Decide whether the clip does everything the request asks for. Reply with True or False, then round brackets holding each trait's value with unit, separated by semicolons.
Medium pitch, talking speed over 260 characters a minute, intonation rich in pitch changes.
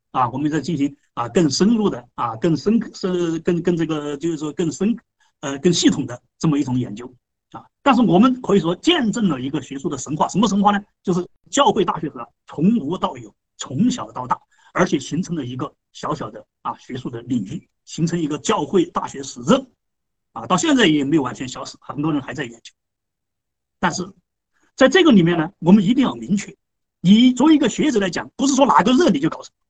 True (175 Hz; 305 characters per minute; 5.9 semitones)